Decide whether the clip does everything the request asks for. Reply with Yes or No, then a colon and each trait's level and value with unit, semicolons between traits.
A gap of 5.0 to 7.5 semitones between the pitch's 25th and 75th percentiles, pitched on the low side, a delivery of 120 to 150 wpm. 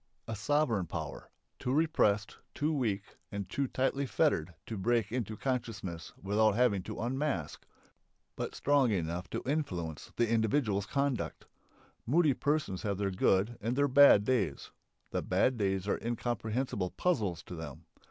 Yes: wide, 5.4 semitones; low, 110 Hz; average, 145 wpm